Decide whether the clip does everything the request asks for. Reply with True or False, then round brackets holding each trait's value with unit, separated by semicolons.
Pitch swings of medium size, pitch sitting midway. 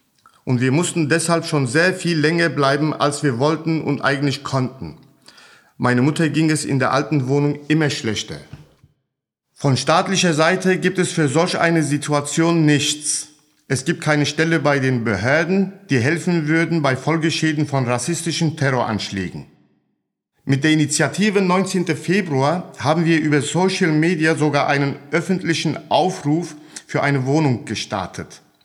True (3.0 semitones; 150 Hz)